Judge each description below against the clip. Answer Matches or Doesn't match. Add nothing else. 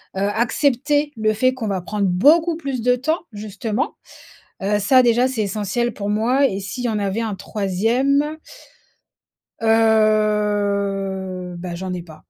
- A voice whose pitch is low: Doesn't match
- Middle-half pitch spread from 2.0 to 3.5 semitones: Doesn't match